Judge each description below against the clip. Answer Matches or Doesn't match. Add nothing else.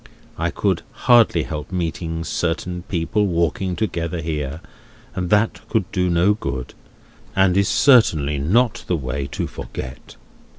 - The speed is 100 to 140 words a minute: Matches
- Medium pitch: Doesn't match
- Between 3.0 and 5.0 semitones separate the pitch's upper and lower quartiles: Matches